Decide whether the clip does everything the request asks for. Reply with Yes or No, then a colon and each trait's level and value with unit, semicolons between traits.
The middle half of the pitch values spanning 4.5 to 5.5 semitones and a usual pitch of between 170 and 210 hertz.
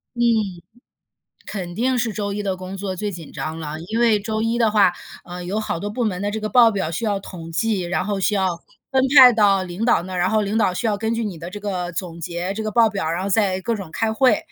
No: average, 3.4 semitones; high, 200 Hz